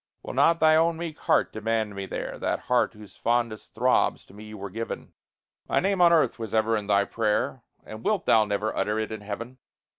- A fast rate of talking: Yes, fast, 210 wpm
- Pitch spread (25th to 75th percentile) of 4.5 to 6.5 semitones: No, average, 3.7 semitones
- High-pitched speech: No, low, 110 Hz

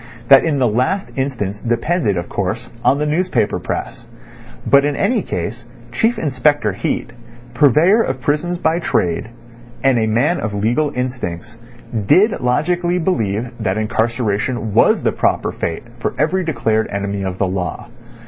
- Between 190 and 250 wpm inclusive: No, average, 150 wpm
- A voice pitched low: Yes, low, 125 Hz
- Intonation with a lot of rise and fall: Yes, wide, 6.3 semitones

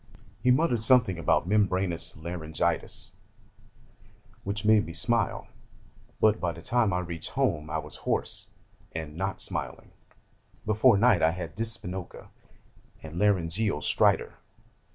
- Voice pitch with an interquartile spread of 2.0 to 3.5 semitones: No, average, 4.7 semitones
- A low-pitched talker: Yes, very low, 90 Hz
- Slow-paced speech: Yes, slow, 125 wpm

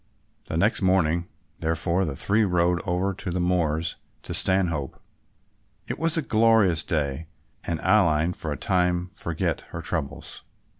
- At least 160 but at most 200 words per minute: No, average, 140 wpm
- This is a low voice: Yes, very low, 90 Hz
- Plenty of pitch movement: No, average, 2.8 semitones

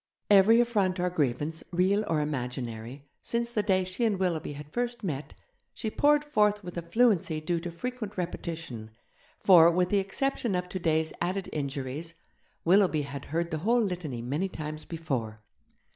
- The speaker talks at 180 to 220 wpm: No, average, 160 wpm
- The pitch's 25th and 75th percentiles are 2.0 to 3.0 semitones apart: No, average, 5.1 semitones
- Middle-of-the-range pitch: Yes, medium, 175 Hz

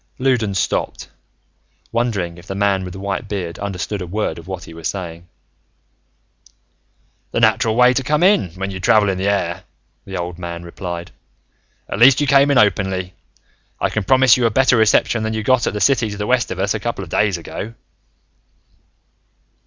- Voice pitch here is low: Yes, low, 100 Hz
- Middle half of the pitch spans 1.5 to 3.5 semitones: No, average, 4.1 semitones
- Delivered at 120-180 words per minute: No, average, 195 wpm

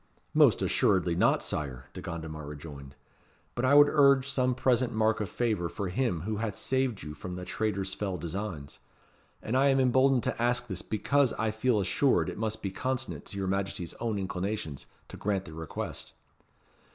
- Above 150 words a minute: Yes, average, 180 wpm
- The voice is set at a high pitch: No, low, 105 Hz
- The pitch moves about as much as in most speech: No, wide, 5.8 semitones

